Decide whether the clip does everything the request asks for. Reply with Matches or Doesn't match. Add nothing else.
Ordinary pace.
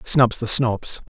Matches